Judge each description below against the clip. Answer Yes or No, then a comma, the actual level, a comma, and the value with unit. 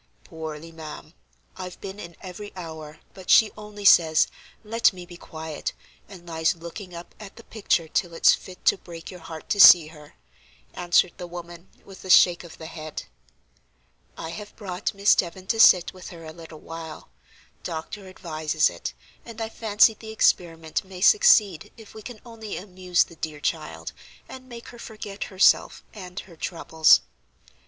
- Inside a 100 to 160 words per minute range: No, average, 170 wpm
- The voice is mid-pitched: Yes, medium, 180 Hz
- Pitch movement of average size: Yes, average, 4.0 semitones